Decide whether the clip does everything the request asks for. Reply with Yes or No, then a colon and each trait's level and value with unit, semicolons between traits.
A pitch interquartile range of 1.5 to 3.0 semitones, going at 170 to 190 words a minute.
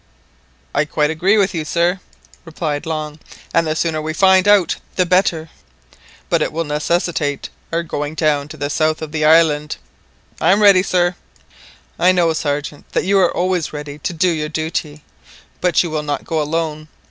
Yes: narrow, 2.6 semitones; average, 180 wpm